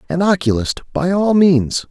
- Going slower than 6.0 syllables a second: Yes, 4.5 syllables/s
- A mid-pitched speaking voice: Yes, medium, 165 Hz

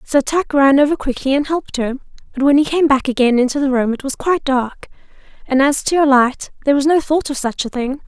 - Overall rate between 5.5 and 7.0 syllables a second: Yes, 6.1 syllables/s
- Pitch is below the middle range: No, very high, 275 Hz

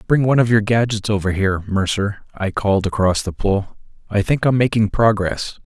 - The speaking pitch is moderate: No, low, 105 Hz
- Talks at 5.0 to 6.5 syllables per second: Yes, 5.5 syllables/s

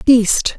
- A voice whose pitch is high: Yes, high, 235 Hz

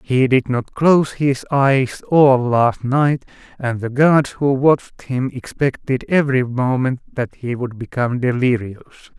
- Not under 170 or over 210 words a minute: No, average, 150 wpm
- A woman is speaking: No, male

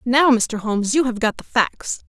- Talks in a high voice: Yes, high, 235 Hz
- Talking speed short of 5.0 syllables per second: Yes, 4.7 syllables/s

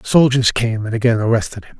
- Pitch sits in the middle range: No, low, 115 Hz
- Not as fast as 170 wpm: No, average, 200 wpm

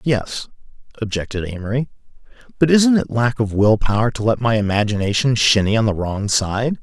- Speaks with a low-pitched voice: Yes, low, 115 Hz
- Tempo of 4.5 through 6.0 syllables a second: Yes, 5.2 syllables/s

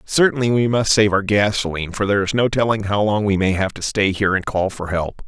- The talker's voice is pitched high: No, low, 105 Hz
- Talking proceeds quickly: Yes, fast, 260 wpm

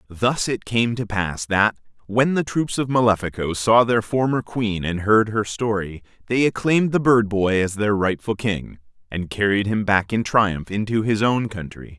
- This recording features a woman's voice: No, male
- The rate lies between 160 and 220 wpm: Yes, average, 190 wpm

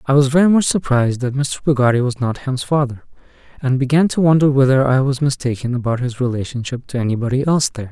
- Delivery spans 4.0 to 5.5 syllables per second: No, 6.5 syllables/s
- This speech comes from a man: Yes, male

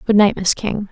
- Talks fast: Yes, fast, 265 wpm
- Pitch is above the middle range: Yes, high, 200 Hz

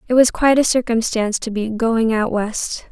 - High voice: Yes, high, 230 Hz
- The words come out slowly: No, fast, 205 wpm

